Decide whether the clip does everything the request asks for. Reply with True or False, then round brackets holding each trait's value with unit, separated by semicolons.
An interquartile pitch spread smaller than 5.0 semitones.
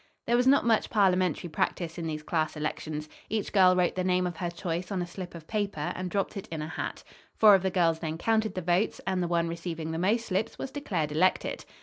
True (3.1 semitones)